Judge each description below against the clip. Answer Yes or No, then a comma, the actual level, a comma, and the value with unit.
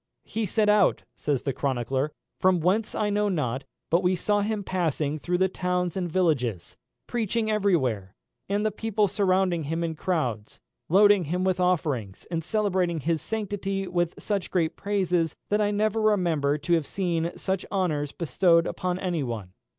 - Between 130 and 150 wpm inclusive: No, average, 170 wpm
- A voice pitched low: No, medium, 180 Hz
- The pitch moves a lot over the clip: No, average, 4.4 semitones